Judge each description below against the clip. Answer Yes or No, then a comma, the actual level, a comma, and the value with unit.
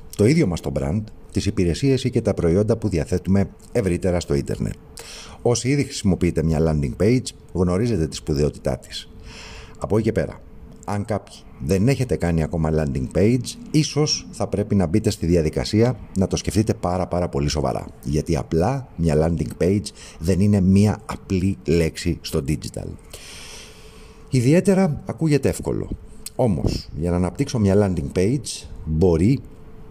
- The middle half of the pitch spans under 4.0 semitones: No, average, 5.0 semitones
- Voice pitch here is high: No, very low, 95 Hz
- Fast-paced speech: No, average, 150 wpm